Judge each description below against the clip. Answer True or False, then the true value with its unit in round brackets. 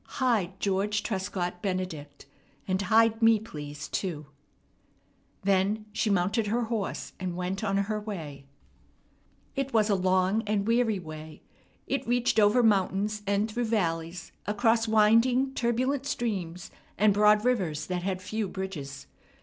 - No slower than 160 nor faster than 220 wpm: False (135 wpm)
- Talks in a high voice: True (205 Hz)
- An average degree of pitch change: True (3.5 semitones)